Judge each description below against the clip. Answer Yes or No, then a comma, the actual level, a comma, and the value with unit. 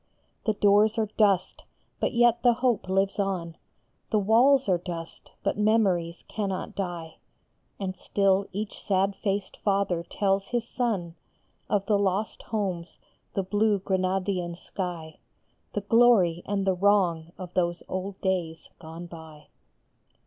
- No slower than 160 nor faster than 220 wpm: No, slow, 135 wpm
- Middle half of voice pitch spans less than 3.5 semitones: Yes, average, 2.9 semitones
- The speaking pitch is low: No, high, 195 Hz